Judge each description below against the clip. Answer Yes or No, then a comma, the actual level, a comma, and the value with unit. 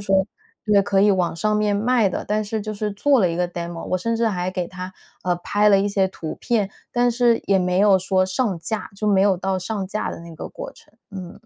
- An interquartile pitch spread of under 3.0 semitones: Yes, narrow, 2.5 semitones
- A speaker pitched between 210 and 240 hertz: No, high, 195 Hz